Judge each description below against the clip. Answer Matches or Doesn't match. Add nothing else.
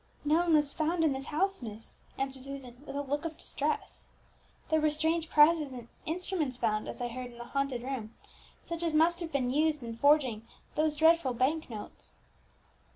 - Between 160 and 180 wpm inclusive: Doesn't match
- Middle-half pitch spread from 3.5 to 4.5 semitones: Matches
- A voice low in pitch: Doesn't match